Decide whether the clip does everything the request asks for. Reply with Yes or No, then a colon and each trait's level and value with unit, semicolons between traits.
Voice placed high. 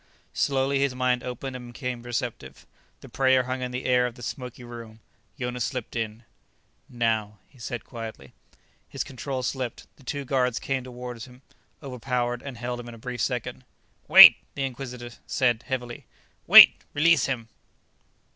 No: low, 125 Hz